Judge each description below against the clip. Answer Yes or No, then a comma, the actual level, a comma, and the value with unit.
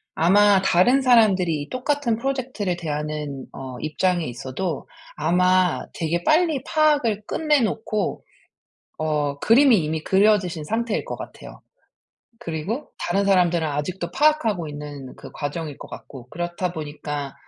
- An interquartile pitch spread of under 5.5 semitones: No, wide, 6.6 semitones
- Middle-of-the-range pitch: Yes, medium, 180 Hz